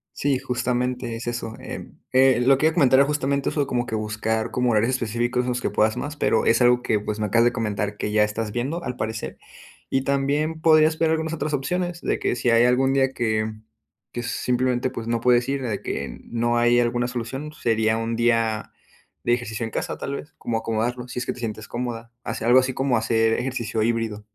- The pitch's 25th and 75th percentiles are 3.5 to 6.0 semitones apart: No, average, 2.7 semitones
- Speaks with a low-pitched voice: Yes, low, 120 Hz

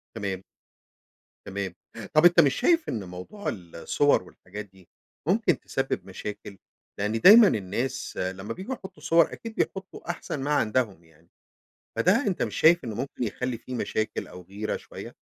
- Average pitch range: No, wide, 8.3 semitones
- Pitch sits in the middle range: No, low, 115 Hz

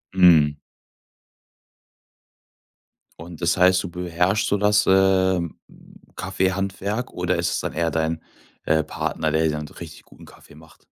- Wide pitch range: No, average, 2.9 semitones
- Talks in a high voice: No, very low, 90 Hz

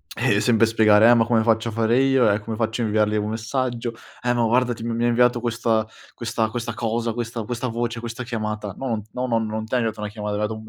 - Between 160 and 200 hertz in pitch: No, low, 115 Hz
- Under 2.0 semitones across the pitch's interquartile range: Yes, narrow, 1.6 semitones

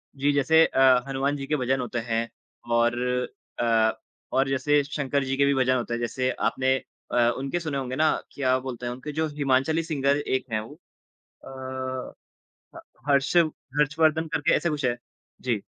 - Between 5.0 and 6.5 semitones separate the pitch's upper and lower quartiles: No, narrow, 2.4 semitones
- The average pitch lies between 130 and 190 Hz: Yes, low, 135 Hz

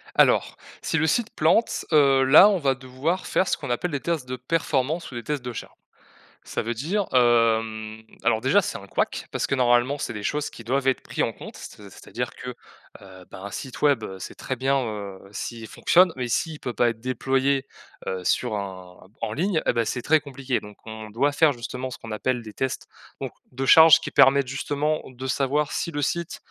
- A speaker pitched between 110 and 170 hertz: Yes, low, 130 Hz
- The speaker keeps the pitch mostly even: No, average, 4.2 semitones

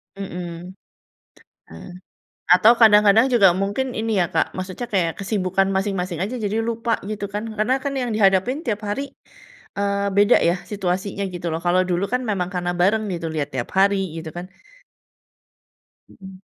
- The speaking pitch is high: Yes, high, 195 Hz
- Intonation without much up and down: No, average, 3.2 semitones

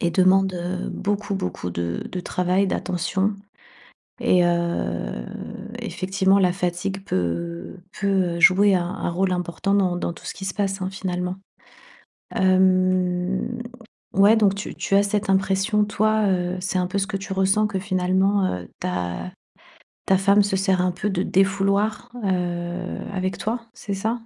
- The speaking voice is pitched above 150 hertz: Yes, high, 190 Hz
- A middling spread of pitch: No, narrow, 1.7 semitones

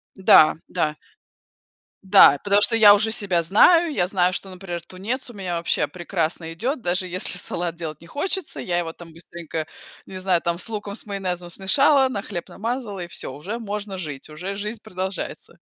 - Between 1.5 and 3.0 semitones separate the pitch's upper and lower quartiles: No, average, 3.4 semitones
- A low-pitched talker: No, medium, 185 Hz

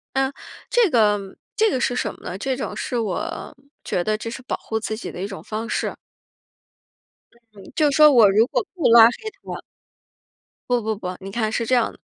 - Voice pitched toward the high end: Yes, high, 230 Hz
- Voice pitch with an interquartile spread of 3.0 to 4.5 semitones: Yes, average, 4.0 semitones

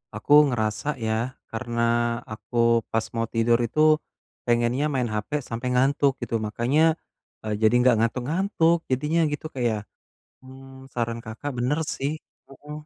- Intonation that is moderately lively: Yes, average, 3.2 semitones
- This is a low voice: Yes, low, 125 Hz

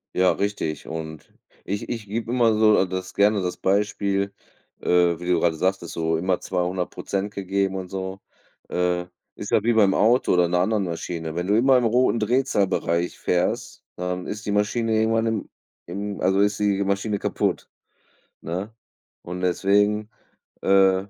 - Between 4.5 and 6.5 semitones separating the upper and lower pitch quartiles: No, average, 2.8 semitones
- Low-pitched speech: Yes, low, 100 Hz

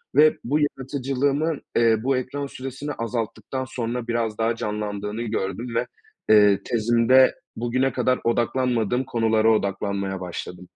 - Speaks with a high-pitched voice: No, low, 120 Hz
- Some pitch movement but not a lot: Yes, average, 3.2 semitones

